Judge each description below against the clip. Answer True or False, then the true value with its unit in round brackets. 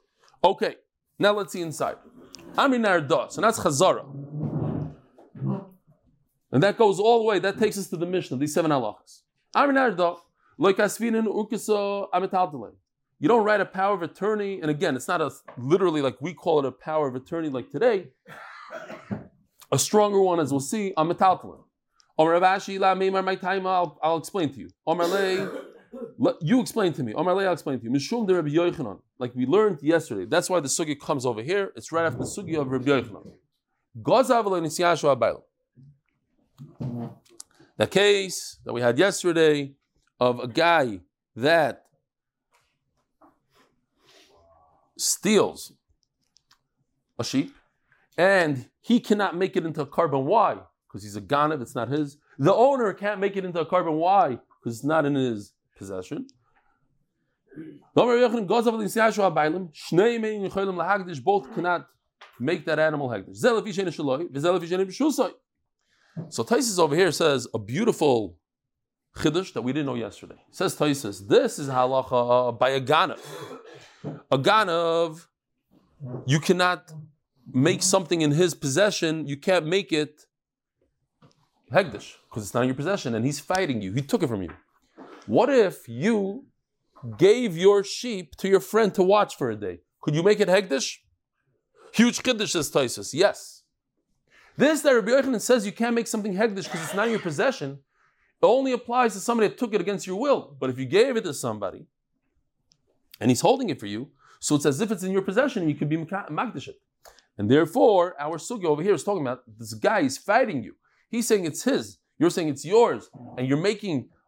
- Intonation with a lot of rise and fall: True (6.2 semitones)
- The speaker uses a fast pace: False (155 wpm)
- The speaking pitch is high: False (175 Hz)